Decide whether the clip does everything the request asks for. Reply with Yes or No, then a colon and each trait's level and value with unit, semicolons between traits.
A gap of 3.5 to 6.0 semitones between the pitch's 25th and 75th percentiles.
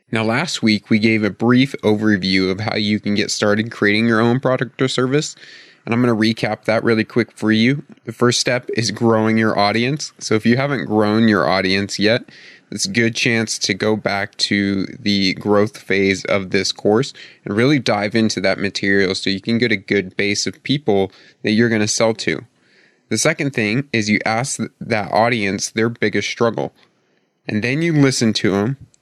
No: average, 2.8 semitones